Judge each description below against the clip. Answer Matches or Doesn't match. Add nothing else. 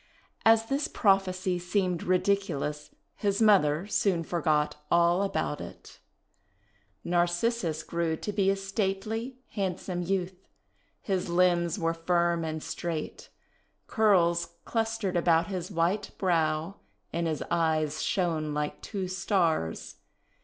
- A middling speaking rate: Doesn't match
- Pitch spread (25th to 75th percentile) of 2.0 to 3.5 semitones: Matches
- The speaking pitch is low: Doesn't match